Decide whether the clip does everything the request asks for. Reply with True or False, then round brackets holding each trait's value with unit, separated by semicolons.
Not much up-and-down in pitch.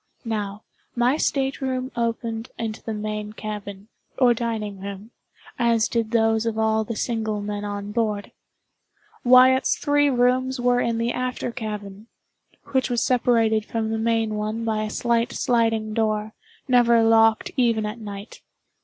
True (2.1 semitones)